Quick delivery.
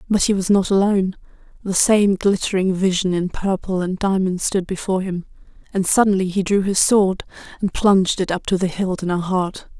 No: average, 195 wpm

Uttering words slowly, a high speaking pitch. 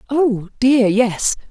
Yes: slow, 120 wpm; high, 235 Hz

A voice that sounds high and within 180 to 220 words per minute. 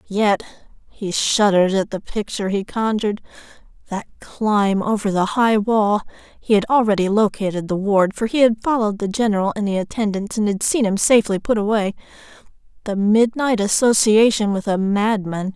No: high, 210 Hz; average, 155 wpm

